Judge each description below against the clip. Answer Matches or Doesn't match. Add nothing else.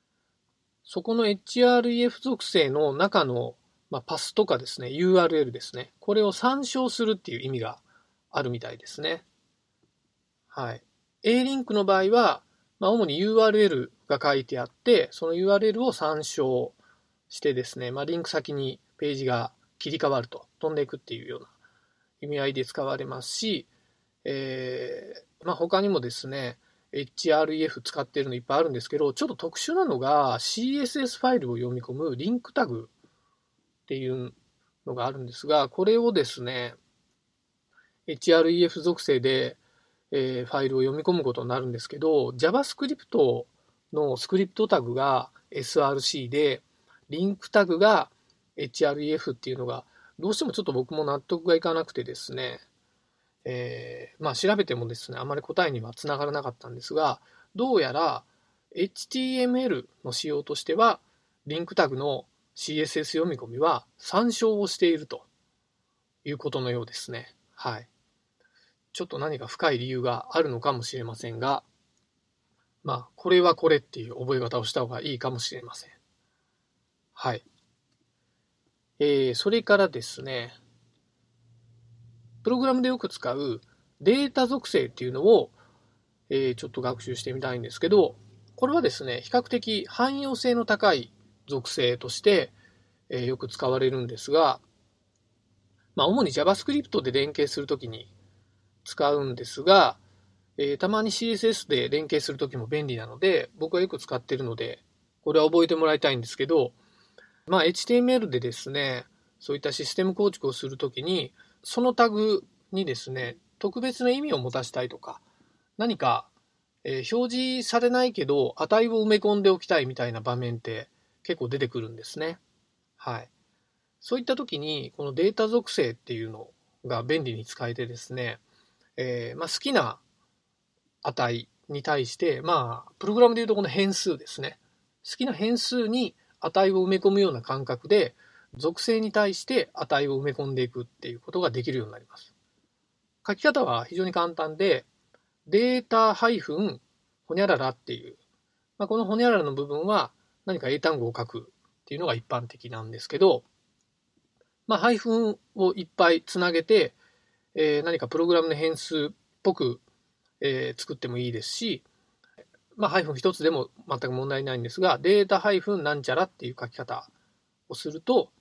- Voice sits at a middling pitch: Matches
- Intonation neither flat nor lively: Doesn't match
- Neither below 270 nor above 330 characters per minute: Matches